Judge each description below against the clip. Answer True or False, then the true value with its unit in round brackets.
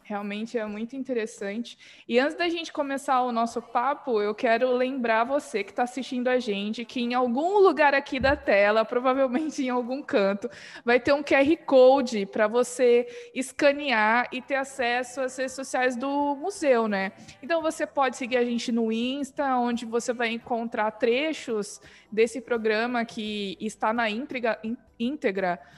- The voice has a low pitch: False (245 Hz)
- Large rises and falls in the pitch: False (3.0 semitones)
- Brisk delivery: False (160 wpm)